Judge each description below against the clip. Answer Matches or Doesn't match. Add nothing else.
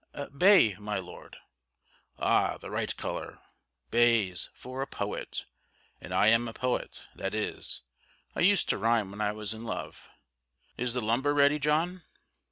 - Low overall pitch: Matches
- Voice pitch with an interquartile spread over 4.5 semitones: Matches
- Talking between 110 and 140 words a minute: Doesn't match